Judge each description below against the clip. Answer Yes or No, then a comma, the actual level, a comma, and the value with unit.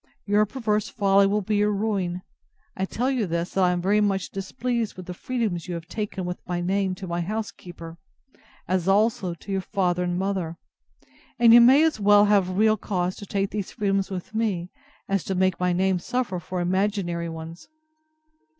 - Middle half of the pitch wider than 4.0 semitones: No, average, 2.8 semitones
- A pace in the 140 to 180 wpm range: No, average, 190 wpm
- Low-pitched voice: No, high, 195 Hz